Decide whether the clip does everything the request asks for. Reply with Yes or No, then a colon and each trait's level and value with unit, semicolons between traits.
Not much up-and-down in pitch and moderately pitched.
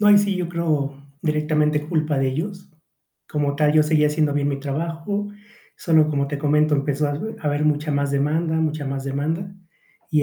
Yes: narrow, 2.0 semitones; medium, 150 Hz